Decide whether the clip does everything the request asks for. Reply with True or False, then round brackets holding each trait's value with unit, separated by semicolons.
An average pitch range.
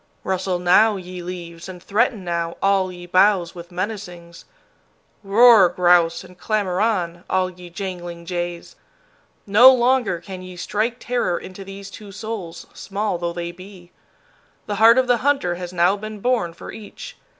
True (3.3 semitones)